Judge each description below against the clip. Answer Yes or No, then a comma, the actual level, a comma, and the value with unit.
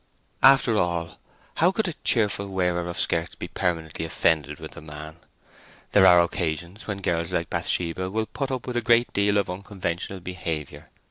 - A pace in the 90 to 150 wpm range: No, average, 175 wpm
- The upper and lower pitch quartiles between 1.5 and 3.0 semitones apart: No, average, 3.7 semitones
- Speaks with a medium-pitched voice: No, very low, 90 Hz